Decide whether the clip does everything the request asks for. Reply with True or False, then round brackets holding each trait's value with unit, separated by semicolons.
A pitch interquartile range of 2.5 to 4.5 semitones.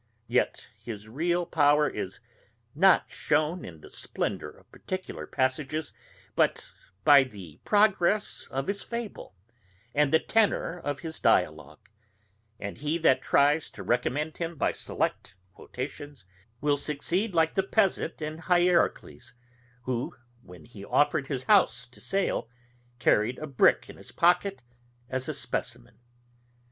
False (5.3 semitones)